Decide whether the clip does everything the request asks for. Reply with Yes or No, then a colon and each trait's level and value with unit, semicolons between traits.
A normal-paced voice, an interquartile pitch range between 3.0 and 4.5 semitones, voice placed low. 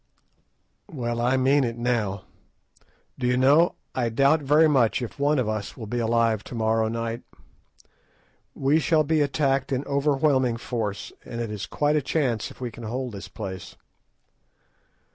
Yes: average, 160 wpm; average, 3.6 semitones; low, 125 Hz